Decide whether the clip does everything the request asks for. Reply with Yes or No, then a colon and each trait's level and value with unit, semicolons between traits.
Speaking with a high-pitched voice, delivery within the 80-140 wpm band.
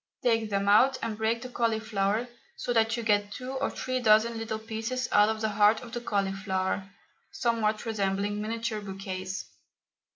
No: high, 220 Hz; average, 165 wpm